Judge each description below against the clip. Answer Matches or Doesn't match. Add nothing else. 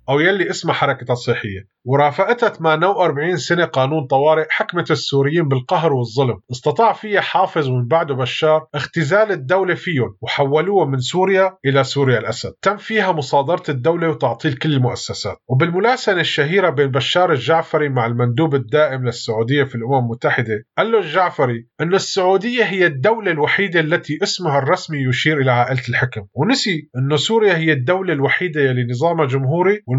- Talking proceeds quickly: Matches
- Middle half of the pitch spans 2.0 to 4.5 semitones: Doesn't match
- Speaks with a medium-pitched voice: Matches